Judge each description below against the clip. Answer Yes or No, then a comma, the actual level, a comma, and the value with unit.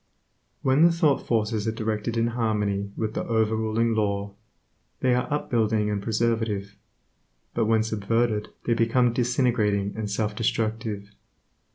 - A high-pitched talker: No, low, 110 Hz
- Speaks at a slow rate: No, average, 145 wpm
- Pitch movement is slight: Yes, narrow, 1.9 semitones